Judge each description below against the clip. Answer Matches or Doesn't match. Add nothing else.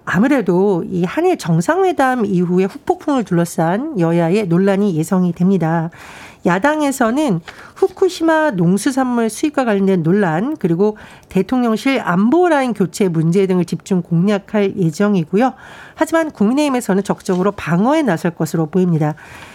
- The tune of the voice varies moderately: Doesn't match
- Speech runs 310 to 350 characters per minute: Matches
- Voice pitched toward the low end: Doesn't match